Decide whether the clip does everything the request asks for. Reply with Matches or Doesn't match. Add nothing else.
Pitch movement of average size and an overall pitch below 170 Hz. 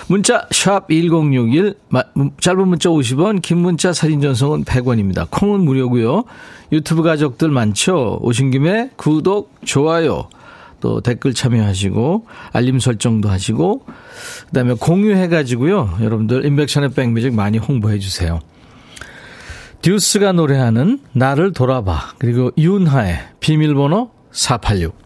Doesn't match